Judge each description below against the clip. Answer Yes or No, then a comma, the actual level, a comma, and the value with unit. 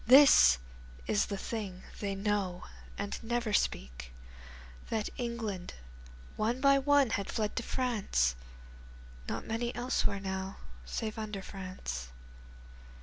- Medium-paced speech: No, slow, 115 wpm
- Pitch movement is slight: No, average, 3.7 semitones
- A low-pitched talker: No, high, 210 Hz